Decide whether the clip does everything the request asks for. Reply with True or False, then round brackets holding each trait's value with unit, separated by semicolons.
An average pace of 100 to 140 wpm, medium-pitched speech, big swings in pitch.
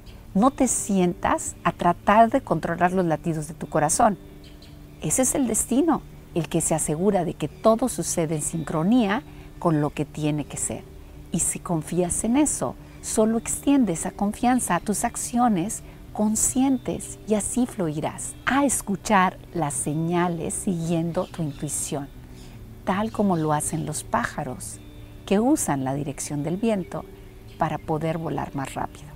False (150 wpm; 175 Hz; 6.0 semitones)